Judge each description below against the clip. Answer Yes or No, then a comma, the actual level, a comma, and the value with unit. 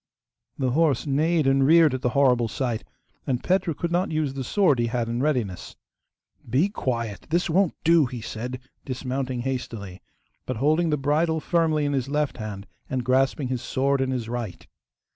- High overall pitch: No, low, 135 Hz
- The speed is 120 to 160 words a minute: No, average, 180 wpm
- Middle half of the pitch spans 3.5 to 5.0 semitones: Yes, average, 4.1 semitones